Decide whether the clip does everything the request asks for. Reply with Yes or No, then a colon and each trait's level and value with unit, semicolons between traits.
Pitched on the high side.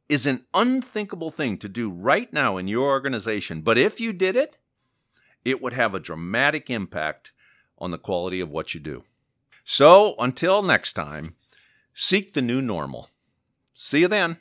No: low, 130 Hz